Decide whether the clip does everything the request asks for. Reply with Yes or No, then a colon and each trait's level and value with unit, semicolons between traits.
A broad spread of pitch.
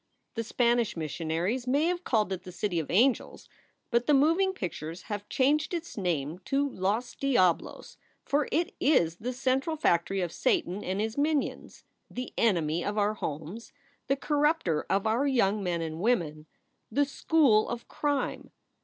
Yes: wide, 7.5 semitones